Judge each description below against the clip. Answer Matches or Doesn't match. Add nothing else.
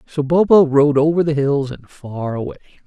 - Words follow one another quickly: Doesn't match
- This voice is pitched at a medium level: Matches